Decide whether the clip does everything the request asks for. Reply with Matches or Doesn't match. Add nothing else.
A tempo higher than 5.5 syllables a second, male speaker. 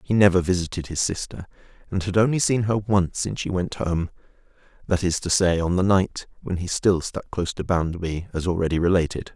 Matches